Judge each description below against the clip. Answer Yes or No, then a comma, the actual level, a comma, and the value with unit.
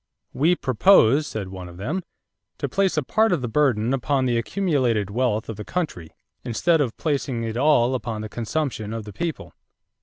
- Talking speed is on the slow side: No, average, 185 wpm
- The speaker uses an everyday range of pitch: No, wide, 5.7 semitones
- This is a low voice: Yes, low, 125 Hz